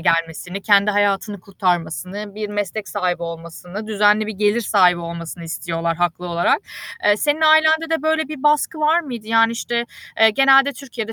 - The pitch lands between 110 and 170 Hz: No, high, 205 Hz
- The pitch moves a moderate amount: No, wide, 5.9 semitones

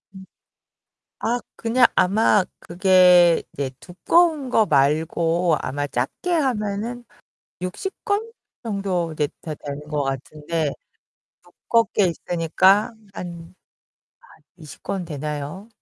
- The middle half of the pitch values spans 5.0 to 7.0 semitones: Yes, wide, 5.6 semitones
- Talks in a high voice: No, medium, 180 Hz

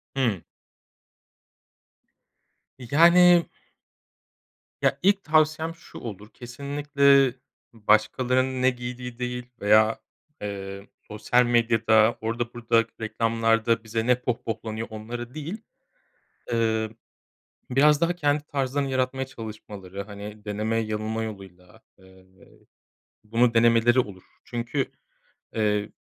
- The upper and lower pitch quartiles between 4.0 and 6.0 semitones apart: No, average, 3.3 semitones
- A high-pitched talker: No, low, 115 Hz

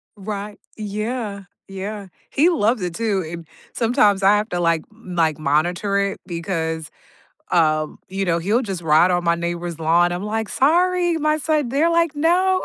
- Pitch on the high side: Yes, high, 200 Hz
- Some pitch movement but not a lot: No, wide, 5.8 semitones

